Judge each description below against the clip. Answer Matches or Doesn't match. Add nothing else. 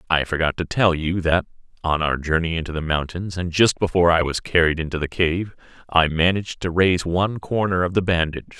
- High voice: Doesn't match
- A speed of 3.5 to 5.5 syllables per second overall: Doesn't match